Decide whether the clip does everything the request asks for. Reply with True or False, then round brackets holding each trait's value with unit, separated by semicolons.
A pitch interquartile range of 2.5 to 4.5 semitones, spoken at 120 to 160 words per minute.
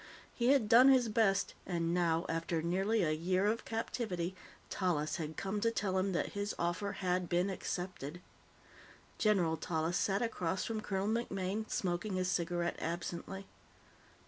True (3.4 semitones; 150 wpm)